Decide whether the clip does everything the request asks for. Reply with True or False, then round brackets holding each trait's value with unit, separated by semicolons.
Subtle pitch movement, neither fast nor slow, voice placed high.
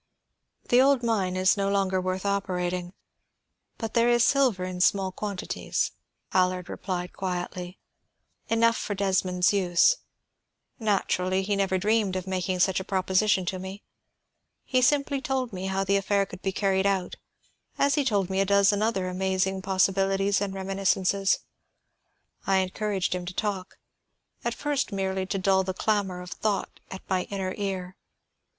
True (1.7 semitones; 155 wpm; 195 Hz)